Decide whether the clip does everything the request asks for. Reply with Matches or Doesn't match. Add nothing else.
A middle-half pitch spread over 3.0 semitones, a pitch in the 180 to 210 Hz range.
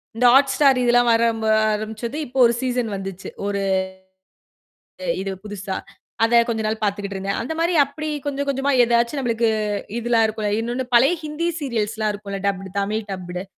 Doesn't match